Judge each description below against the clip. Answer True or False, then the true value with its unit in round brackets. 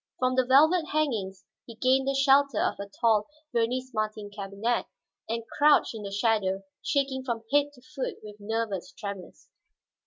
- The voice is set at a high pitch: True (230 Hz)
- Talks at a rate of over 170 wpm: False (160 wpm)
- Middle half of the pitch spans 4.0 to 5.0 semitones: True (4.5 semitones)